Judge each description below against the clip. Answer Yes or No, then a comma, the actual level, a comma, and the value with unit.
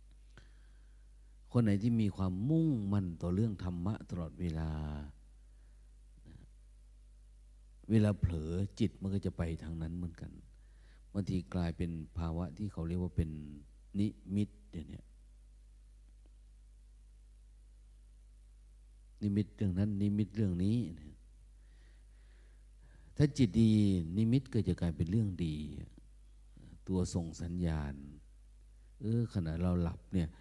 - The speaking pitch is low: Yes, very low, 85 Hz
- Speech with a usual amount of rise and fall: No, wide, 8.7 semitones